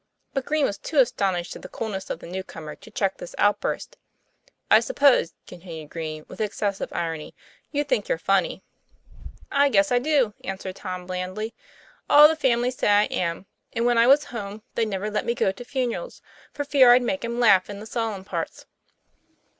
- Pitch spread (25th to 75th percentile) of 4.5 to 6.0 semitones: Yes, wide, 5.4 semitones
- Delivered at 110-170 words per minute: No, average, 190 wpm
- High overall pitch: Yes, high, 220 Hz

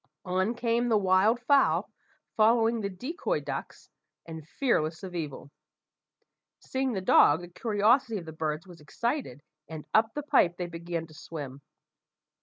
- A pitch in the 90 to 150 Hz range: No, high, 190 Hz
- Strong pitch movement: Yes, wide, 6.2 semitones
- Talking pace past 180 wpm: No, average, 150 wpm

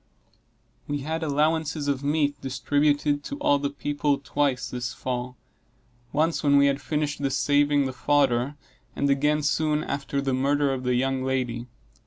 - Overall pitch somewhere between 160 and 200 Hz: No, medium, 145 Hz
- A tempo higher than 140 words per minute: Yes, average, 160 wpm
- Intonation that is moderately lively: No, narrow, 1.7 semitones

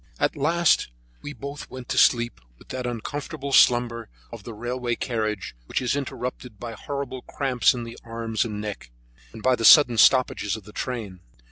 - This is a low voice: Yes, low, 120 Hz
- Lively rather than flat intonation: No, narrow, 2.5 semitones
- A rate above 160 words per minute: Yes, average, 175 wpm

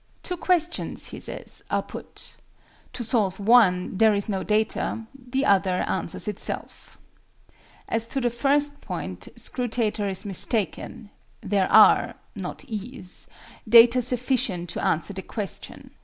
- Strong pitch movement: No, average, 4.0 semitones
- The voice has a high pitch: Yes, high, 220 Hz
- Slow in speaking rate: Yes, slow, 130 wpm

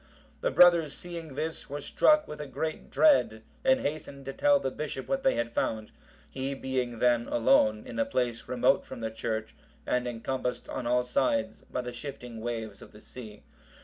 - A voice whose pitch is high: No, low, 130 Hz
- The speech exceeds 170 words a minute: Yes, average, 185 wpm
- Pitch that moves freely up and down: No, average, 4.4 semitones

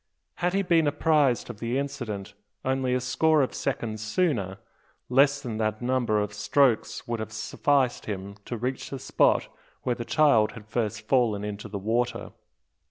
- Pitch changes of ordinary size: Yes, average, 4.1 semitones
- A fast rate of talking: No, average, 165 wpm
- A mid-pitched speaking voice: No, low, 120 Hz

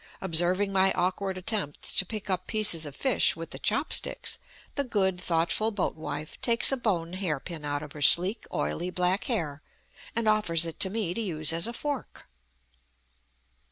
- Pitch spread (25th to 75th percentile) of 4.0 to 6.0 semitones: Yes, average, 4.4 semitones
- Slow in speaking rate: No, average, 180 wpm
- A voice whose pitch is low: No, medium, 185 Hz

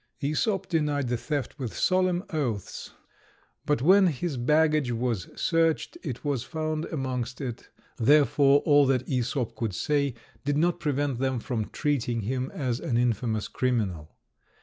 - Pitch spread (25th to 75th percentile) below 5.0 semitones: Yes, average, 3.9 semitones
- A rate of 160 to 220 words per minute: No, average, 145 wpm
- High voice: No, low, 135 Hz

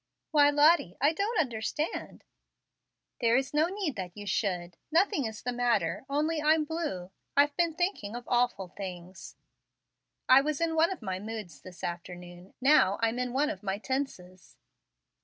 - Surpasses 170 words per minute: No, average, 165 wpm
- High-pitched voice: Yes, high, 245 Hz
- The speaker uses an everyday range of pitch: No, wide, 8.1 semitones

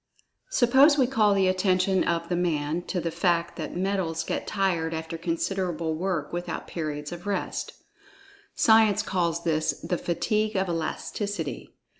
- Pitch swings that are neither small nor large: Yes, average, 3.1 semitones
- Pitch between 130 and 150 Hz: No, medium, 175 Hz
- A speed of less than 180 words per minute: Yes, average, 150 wpm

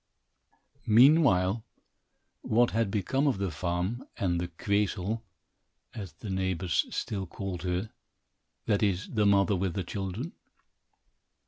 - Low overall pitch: Yes, low, 100 Hz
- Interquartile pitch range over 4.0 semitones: No, average, 3.3 semitones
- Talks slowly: Yes, slow, 120 wpm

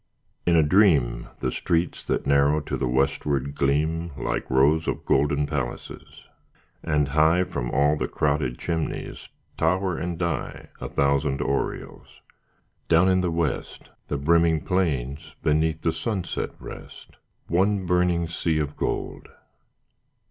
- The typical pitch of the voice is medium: No, very low, 75 Hz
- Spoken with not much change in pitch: No, average, 3.3 semitones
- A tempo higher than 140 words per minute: No, slow, 135 wpm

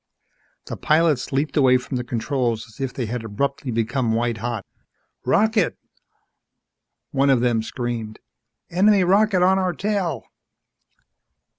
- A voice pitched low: Yes, low, 130 Hz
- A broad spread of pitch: Yes, wide, 6.8 semitones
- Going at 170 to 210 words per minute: No, slow, 135 wpm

